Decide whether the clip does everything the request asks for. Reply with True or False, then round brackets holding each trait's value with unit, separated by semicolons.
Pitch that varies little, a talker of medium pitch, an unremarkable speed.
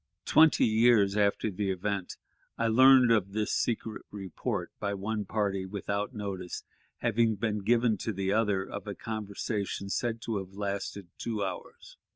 False (2.2 semitones; 105 Hz; 155 wpm)